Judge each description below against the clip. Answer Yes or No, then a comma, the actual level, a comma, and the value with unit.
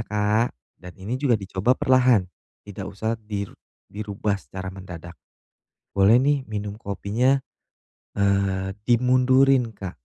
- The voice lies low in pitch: Yes, low, 105 Hz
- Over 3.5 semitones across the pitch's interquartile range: Yes, average, 4.3 semitones